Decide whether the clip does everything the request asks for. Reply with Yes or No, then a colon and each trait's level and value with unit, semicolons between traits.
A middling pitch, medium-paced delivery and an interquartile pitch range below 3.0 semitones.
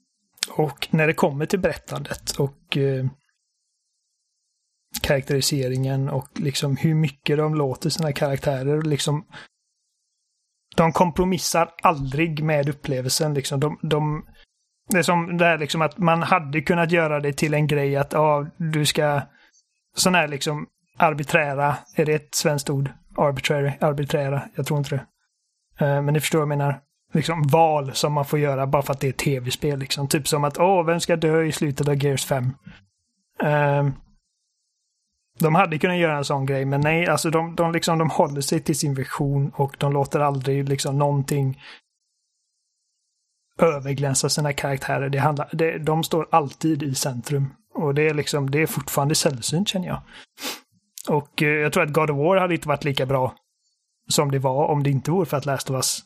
Yes: medium, 150 Hz; average, 175 wpm; narrow, 2.4 semitones